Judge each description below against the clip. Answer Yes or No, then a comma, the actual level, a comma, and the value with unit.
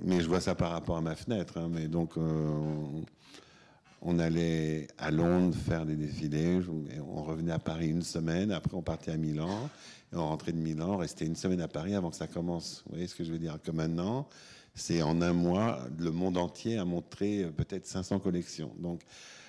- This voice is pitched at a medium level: No, very low, 85 Hz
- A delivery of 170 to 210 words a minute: Yes, average, 205 wpm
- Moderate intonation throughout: No, narrow, 1.8 semitones